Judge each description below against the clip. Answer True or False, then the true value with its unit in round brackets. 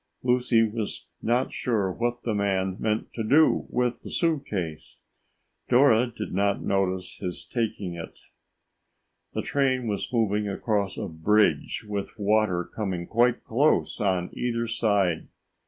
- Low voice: True (110 Hz)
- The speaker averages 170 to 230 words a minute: False (140 wpm)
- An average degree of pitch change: True (3.7 semitones)